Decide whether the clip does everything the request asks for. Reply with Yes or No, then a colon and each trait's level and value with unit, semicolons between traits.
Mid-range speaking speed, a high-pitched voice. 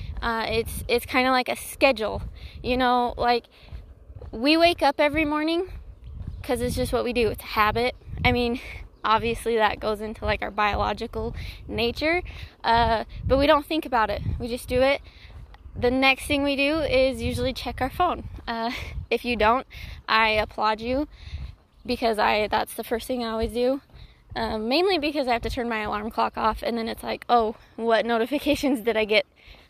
Yes: average, 185 wpm; high, 240 Hz